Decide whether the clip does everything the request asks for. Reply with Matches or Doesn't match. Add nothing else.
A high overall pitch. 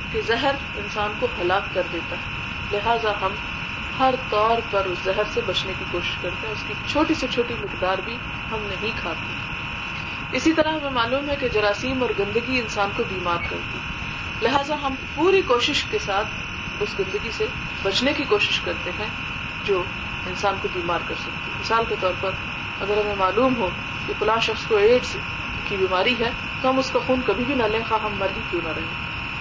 Matches